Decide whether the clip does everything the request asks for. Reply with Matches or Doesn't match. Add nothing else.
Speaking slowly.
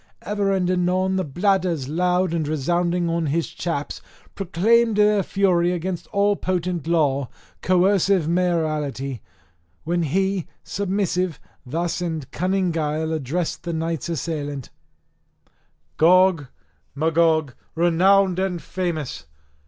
Matches